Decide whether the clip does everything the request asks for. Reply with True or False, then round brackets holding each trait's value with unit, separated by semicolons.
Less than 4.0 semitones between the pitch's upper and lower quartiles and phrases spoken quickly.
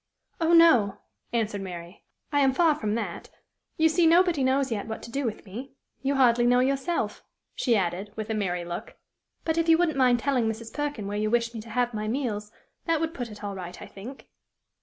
False (5.1 semitones; 215 wpm)